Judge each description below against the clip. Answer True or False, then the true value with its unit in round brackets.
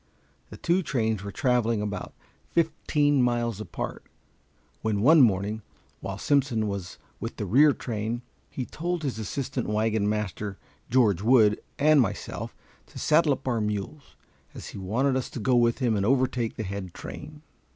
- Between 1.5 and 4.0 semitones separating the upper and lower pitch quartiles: False (4.6 semitones)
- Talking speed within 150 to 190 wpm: True (160 wpm)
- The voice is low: True (115 Hz)